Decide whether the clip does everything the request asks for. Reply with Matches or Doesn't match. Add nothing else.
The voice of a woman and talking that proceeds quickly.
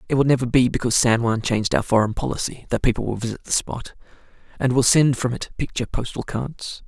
Doesn't match